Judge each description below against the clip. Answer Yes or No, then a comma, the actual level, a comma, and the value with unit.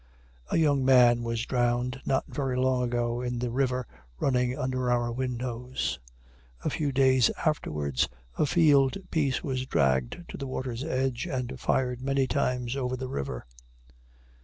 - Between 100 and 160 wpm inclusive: Yes, average, 150 wpm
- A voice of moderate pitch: No, low, 130 Hz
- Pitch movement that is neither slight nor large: No, narrow, 1.7 semitones